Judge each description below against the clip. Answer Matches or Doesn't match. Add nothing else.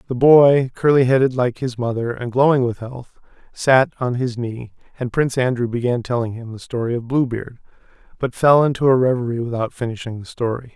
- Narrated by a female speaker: Doesn't match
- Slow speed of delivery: Doesn't match